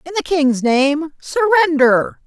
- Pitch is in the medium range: No, very high, 310 Hz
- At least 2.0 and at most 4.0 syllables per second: Yes, 3.5 syllables/s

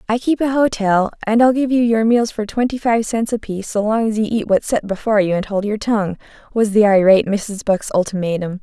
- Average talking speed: No, fast, 235 wpm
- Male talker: No, female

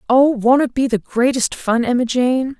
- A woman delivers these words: Yes, female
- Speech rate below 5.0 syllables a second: Yes, 4.6 syllables/s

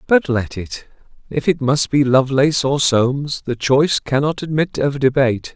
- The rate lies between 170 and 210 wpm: No, average, 160 wpm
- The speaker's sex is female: No, male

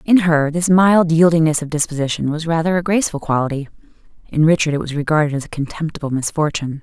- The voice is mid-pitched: Yes, medium, 155 Hz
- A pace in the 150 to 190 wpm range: Yes, average, 185 wpm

